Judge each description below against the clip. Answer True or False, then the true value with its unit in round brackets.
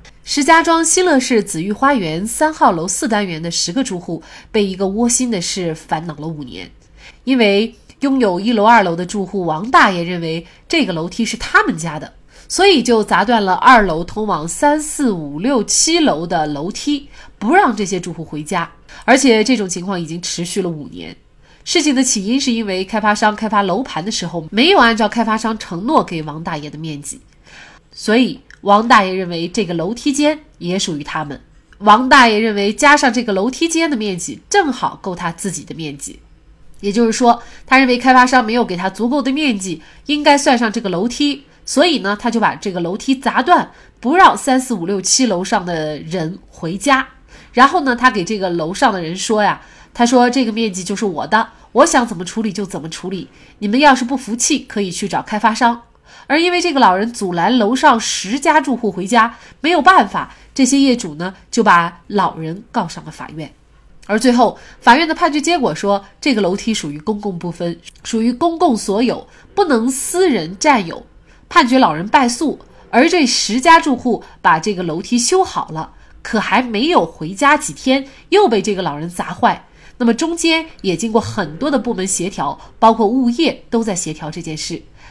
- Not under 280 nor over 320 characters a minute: True (285 characters per minute)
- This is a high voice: True (220 Hz)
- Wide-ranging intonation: True (6.3 semitones)